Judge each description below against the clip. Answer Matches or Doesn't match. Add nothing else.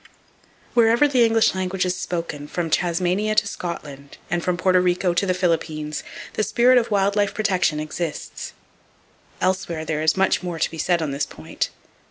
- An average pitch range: Matches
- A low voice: Doesn't match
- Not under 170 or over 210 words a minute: Matches